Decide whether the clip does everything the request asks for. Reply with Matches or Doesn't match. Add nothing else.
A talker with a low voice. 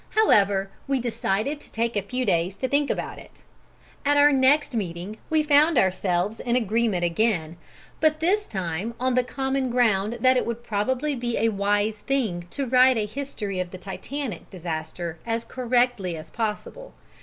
Doesn't match